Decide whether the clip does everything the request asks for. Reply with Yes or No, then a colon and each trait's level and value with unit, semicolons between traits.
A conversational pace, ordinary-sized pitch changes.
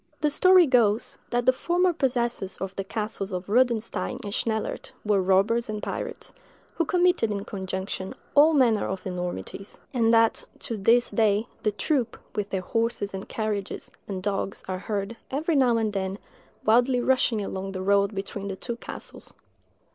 Yes: average, 165 wpm; average, 3.7 semitones